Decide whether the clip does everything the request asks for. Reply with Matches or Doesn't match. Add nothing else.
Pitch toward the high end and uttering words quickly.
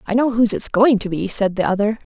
Matches